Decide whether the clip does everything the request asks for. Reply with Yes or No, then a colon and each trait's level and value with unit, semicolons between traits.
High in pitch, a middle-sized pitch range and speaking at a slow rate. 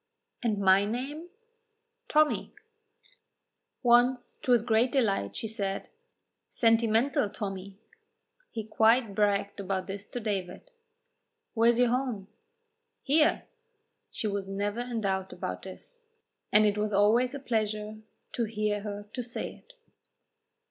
Yes: high, 215 Hz; average, 3.2 semitones; slow, 125 wpm